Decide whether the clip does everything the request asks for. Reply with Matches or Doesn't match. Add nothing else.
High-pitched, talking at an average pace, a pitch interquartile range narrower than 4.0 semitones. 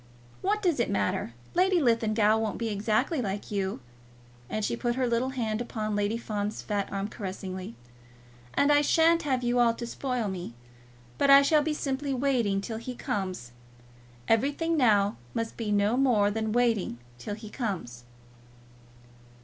Doesn't match